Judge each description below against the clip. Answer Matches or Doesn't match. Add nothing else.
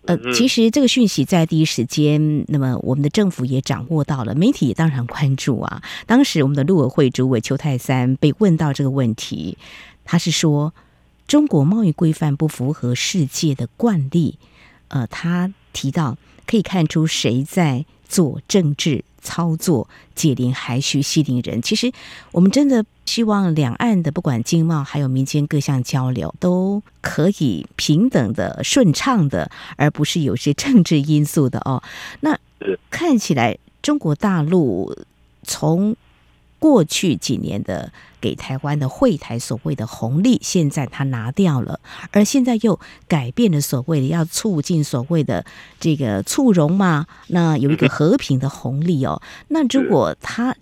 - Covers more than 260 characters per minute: Doesn't match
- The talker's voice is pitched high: Doesn't match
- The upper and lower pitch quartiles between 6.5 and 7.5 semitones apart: Doesn't match